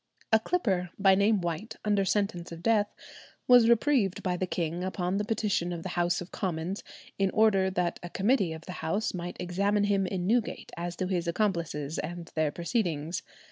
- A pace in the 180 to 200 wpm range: Yes, average, 185 wpm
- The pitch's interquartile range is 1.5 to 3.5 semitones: Yes, average, 3.1 semitones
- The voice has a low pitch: No, medium, 185 Hz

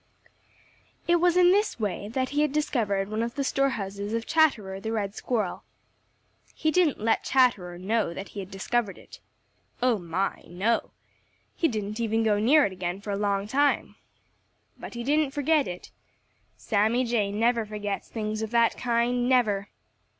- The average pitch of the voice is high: Yes, high, 225 Hz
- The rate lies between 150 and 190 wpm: Yes, average, 170 wpm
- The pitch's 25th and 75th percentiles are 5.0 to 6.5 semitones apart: No, average, 4.3 semitones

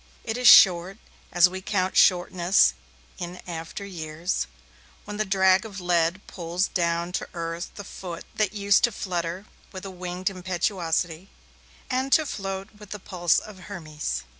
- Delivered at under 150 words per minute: No, average, 155 wpm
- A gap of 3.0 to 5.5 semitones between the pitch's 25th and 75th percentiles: No, narrow, 2.4 semitones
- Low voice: No, medium, 185 Hz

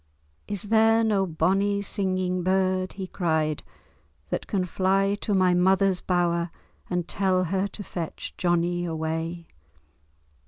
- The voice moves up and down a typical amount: No, narrow, 2.1 semitones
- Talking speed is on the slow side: Yes, slow, 125 wpm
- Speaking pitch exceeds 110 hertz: Yes, medium, 185 Hz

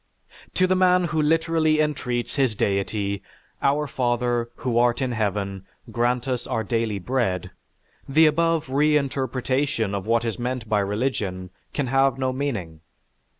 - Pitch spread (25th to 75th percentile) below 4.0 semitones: No, average, 4.7 semitones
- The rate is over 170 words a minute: No, average, 150 wpm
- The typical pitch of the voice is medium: No, low, 125 Hz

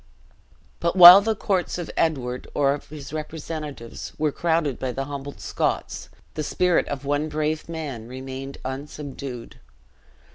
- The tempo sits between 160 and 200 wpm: No, average, 140 wpm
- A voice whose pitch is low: No, medium, 145 Hz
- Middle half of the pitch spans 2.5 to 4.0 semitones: Yes, average, 3.0 semitones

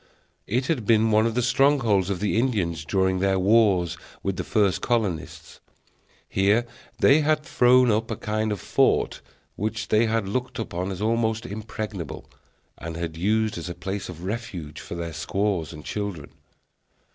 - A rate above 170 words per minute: No, average, 165 wpm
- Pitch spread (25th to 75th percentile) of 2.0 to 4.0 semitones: Yes, average, 3.7 semitones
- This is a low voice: Yes, low, 105 Hz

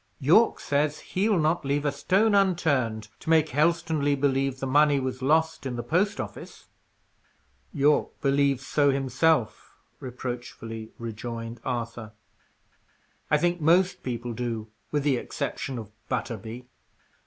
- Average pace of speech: No, slow, 130 wpm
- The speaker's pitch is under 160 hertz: Yes, medium, 140 Hz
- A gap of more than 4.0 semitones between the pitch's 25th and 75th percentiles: Yes, average, 4.7 semitones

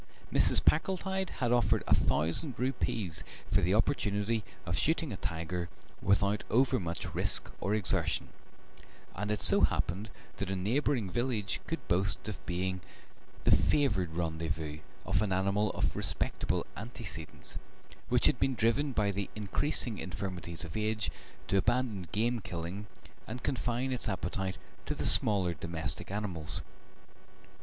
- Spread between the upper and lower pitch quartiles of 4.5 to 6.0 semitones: Yes, average, 5.1 semitones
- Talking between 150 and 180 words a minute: No, slow, 135 wpm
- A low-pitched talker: Yes, low, 100 Hz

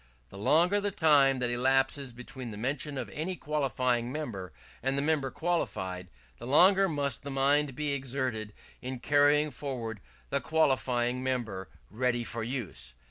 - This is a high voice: No, low, 130 Hz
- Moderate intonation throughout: Yes, average, 3.5 semitones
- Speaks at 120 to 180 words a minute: Yes, average, 150 wpm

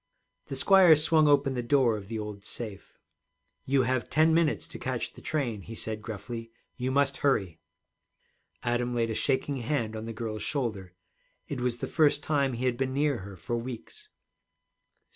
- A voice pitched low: Yes, low, 125 Hz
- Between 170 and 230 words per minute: Yes, average, 180 wpm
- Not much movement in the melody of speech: No, average, 4.1 semitones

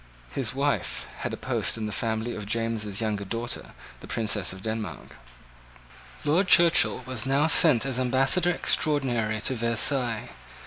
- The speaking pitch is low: Yes, low, 120 Hz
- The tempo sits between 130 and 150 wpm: Yes, average, 145 wpm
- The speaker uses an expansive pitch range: No, average, 3.8 semitones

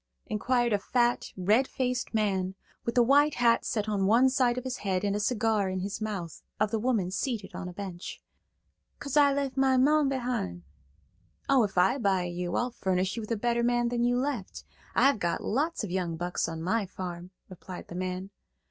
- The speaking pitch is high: Yes, high, 215 Hz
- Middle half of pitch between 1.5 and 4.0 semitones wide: No, average, 5.0 semitones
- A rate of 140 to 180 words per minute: No, average, 200 wpm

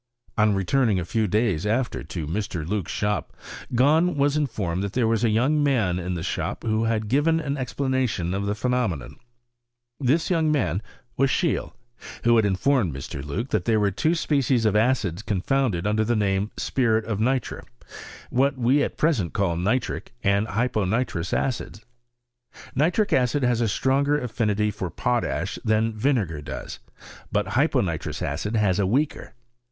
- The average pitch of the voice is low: Yes, low, 110 Hz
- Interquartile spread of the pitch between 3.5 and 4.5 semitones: No, average, 5.0 semitones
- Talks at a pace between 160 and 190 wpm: Yes, average, 170 wpm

